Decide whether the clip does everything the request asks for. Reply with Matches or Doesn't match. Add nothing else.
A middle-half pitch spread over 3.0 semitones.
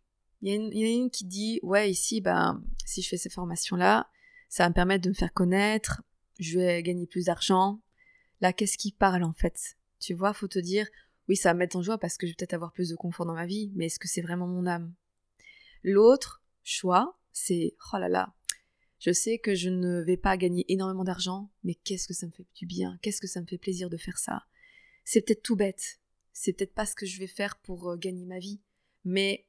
Doesn't match